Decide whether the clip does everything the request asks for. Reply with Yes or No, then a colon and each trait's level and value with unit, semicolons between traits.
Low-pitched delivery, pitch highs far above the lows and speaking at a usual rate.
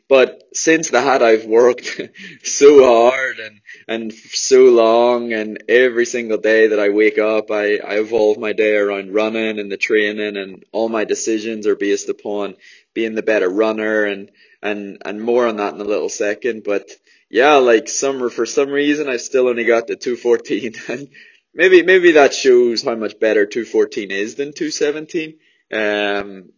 Yes: low, 115 Hz; wide, 5.7 semitones; average, 180 wpm